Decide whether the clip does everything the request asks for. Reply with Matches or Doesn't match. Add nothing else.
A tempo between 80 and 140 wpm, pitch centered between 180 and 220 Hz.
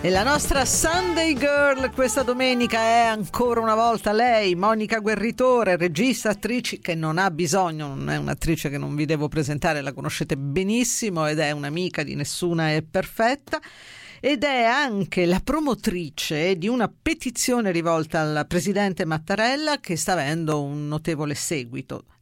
Doesn't match